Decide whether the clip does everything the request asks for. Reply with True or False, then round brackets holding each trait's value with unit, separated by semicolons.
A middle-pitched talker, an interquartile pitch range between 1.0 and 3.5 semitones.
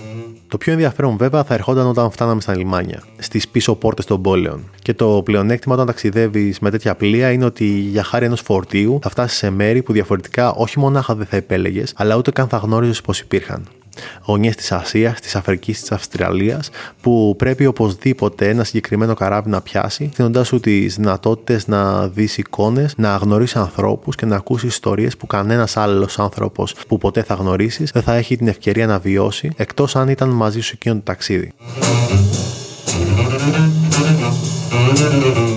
False (110 Hz; 3.2 semitones)